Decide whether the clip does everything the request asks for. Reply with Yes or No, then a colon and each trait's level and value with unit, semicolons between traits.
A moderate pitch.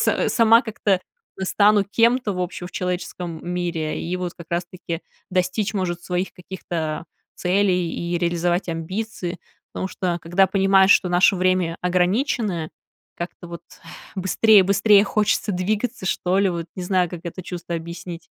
Yes: medium, 180 Hz